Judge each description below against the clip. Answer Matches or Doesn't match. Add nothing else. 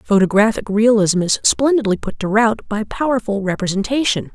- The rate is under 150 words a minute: Matches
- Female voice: Matches